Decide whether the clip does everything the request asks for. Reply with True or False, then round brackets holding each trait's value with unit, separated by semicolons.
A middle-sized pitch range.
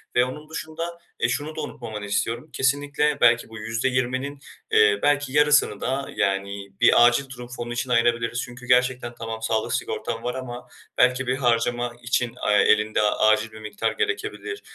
True (3.4 semitones)